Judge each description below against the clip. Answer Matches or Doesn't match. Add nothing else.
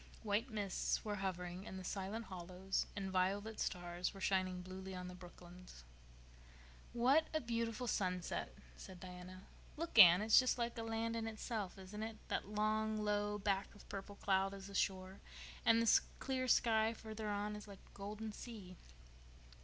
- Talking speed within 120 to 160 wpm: Doesn't match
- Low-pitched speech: Doesn't match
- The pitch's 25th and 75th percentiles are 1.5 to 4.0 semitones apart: Matches